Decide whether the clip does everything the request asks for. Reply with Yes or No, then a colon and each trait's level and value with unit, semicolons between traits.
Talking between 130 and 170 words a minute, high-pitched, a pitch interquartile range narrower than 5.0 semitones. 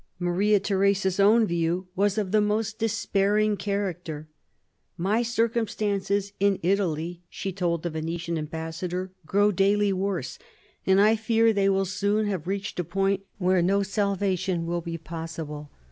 Yes: average, 145 wpm; high, 195 Hz; average, 2.9 semitones